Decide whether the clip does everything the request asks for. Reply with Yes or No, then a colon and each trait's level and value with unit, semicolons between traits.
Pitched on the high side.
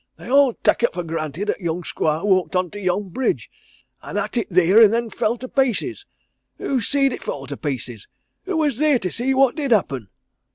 Yes: high, 210 Hz